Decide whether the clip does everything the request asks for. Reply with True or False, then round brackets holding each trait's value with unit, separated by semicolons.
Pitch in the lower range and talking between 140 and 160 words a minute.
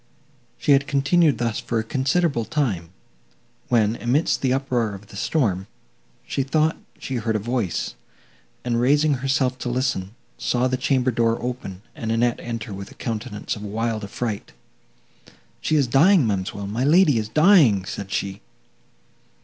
True (120 Hz; 155 wpm)